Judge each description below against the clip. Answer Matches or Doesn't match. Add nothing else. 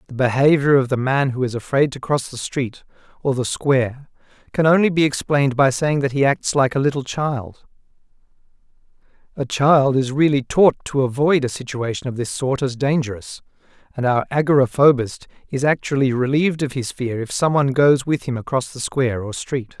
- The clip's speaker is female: Doesn't match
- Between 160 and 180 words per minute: Doesn't match